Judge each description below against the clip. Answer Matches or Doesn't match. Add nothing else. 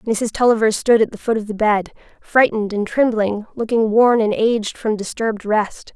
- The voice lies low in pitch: Doesn't match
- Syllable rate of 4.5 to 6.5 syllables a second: Matches